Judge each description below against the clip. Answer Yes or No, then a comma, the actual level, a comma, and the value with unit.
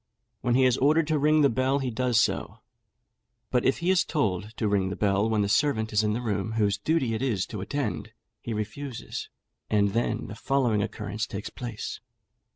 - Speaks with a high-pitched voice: No, low, 115 Hz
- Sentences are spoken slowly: No, average, 200 wpm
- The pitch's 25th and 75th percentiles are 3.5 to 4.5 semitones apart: Yes, average, 4.2 semitones